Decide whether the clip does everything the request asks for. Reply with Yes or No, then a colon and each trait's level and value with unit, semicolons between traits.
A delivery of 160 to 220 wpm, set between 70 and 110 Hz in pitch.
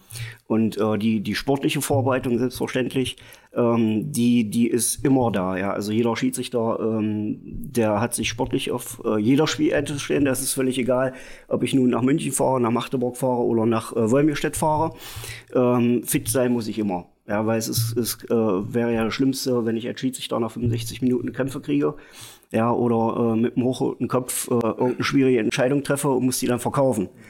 No: fast, 190 wpm; low, 120 Hz